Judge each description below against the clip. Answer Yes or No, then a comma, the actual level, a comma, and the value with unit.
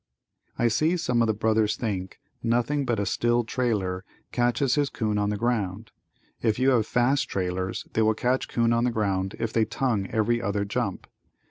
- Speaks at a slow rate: No, average, 190 wpm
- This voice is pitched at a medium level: No, low, 115 Hz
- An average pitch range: Yes, average, 3.0 semitones